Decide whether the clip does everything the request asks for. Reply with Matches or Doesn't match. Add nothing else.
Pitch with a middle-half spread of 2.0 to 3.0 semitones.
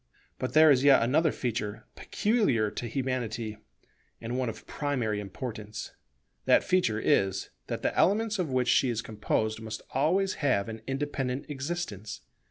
Doesn't match